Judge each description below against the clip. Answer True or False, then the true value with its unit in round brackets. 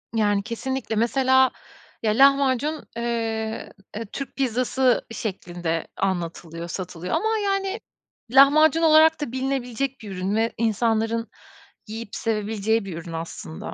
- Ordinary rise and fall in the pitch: True (5.0 semitones)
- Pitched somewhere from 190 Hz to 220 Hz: False (230 Hz)